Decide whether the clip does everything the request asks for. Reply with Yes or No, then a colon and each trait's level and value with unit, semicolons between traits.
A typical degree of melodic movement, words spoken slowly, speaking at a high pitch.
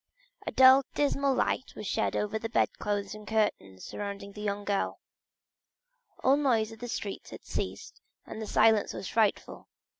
No: average, 3.0 semitones; average, 170 wpm; high, 215 Hz